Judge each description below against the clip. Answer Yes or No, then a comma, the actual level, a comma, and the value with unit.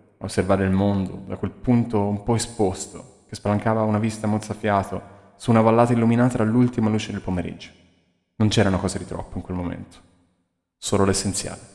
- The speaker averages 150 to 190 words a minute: Yes, average, 165 wpm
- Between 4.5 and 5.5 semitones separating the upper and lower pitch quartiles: No, average, 2.9 semitones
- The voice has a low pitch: Yes, low, 100 Hz